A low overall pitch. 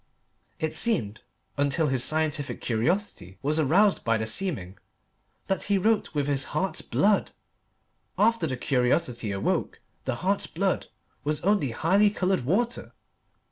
No: medium, 155 Hz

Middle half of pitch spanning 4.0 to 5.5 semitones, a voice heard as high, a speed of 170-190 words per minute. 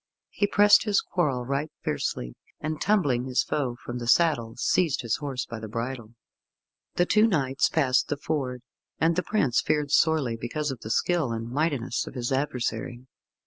No: average, 4.7 semitones; low, 135 Hz; average, 175 wpm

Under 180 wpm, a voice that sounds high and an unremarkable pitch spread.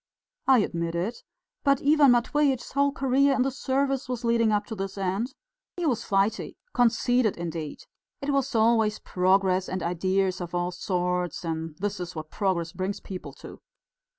No: average, 165 wpm; high, 205 Hz; wide, 6.0 semitones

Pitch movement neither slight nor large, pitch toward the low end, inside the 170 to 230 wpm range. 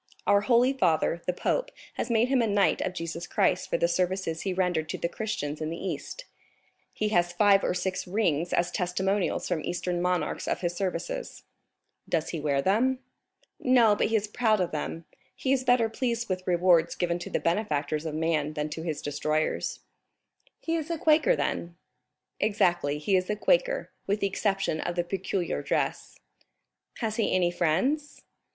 No: average, 4.6 semitones; medium, 185 Hz; average, 180 wpm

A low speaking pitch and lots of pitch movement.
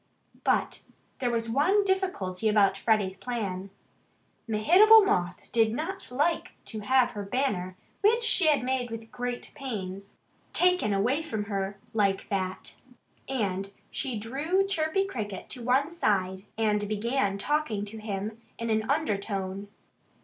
No: high, 225 Hz; wide, 6.0 semitones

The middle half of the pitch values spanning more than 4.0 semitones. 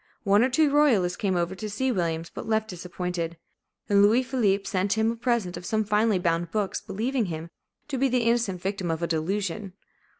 Yes: average, 4.4 semitones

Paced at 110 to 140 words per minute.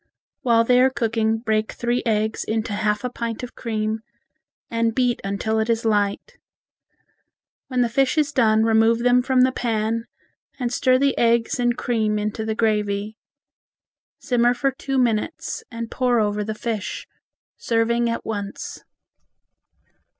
No: average, 150 wpm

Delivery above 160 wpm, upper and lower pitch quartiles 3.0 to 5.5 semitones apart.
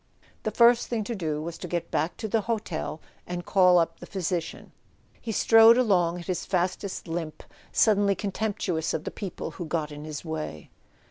Yes: average, 185 wpm; average, 4.2 semitones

